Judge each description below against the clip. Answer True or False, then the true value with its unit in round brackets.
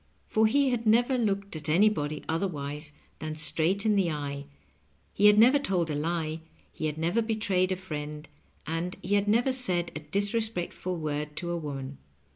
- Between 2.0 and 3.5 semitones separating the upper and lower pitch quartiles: False (5.5 semitones)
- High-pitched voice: False (175 Hz)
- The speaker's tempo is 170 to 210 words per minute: True (175 wpm)